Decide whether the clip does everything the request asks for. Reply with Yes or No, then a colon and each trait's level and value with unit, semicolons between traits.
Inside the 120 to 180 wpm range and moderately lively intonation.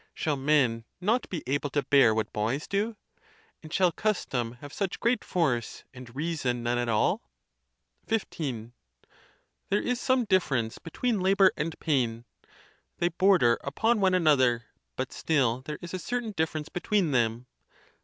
No: average, 155 wpm; wide, 7.6 semitones